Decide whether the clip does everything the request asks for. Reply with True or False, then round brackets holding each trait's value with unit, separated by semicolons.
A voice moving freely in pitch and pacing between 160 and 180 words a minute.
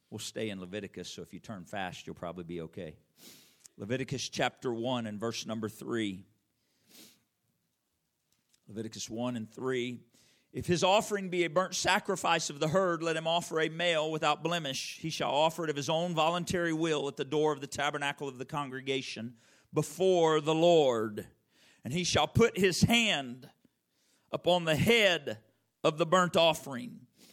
True (6.4 semitones; 165 wpm)